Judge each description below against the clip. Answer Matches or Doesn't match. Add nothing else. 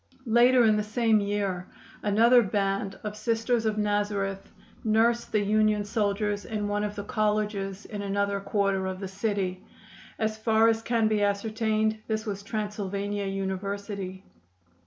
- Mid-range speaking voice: Doesn't match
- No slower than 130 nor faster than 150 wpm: Matches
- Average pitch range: Doesn't match